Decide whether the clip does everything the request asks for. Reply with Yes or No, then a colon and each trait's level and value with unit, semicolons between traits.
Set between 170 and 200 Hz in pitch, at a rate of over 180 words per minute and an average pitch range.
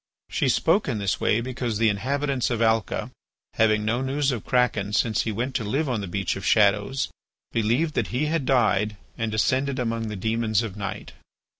No: low, 115 Hz; average, 190 wpm; average, 3.5 semitones